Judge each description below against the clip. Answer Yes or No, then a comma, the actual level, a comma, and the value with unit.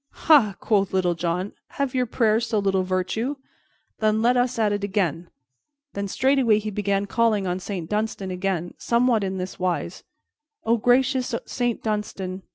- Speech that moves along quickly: No, average, 160 wpm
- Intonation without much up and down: No, average, 3.7 semitones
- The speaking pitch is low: No, high, 210 Hz